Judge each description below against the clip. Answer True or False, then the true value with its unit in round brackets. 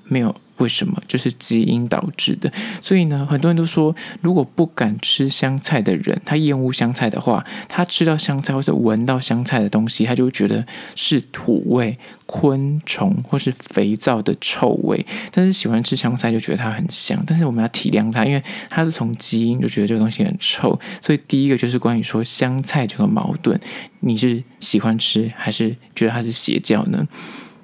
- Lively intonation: True (6.1 semitones)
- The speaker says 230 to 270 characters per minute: False (290 characters per minute)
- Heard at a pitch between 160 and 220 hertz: False (130 Hz)